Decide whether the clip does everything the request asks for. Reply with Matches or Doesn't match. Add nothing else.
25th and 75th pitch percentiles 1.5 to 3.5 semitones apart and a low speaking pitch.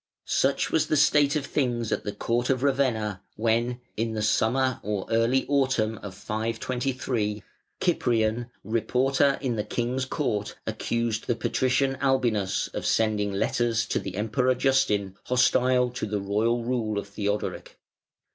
Matches